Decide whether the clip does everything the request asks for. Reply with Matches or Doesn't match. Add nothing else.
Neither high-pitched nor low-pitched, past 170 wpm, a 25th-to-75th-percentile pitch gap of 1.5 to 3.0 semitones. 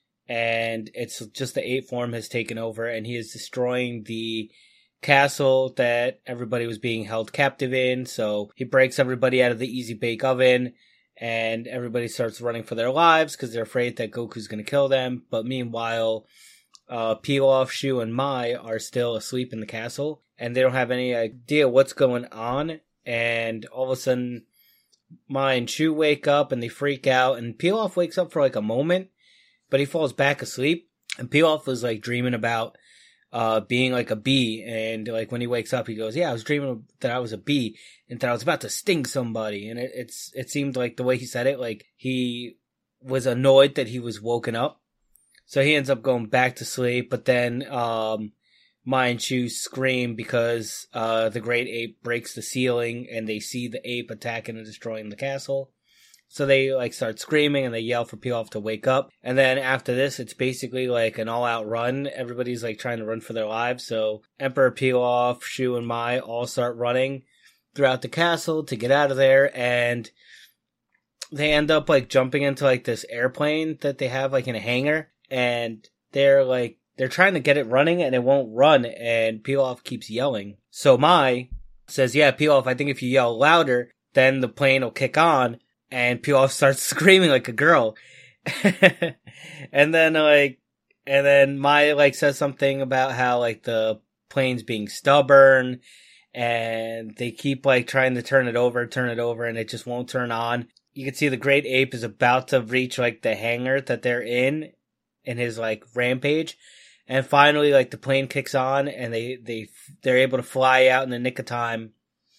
Doesn't match